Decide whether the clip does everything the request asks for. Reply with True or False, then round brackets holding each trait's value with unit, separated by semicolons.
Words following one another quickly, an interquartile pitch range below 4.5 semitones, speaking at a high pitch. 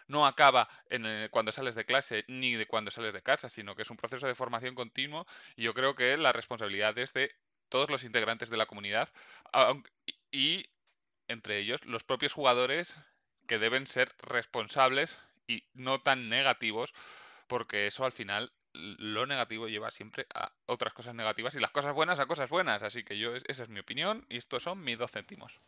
False (195 wpm; 3.1 semitones; 125 Hz)